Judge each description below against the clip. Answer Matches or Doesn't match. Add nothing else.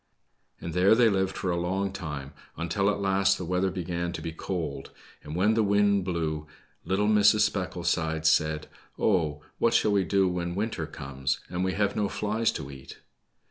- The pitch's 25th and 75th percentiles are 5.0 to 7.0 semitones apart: Doesn't match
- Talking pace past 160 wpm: Matches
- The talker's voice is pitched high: Doesn't match